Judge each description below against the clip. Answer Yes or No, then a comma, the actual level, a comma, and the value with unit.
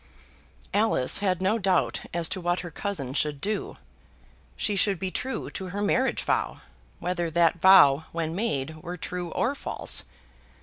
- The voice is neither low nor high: Yes, medium, 180 Hz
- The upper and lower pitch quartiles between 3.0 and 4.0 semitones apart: Yes, average, 3.7 semitones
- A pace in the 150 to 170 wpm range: Yes, average, 160 wpm